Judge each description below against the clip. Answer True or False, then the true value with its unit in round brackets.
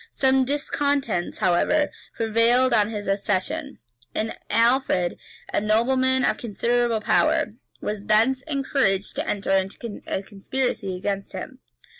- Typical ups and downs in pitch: True (4.6 semitones)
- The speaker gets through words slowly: True (120 wpm)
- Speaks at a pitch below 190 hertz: False (230 Hz)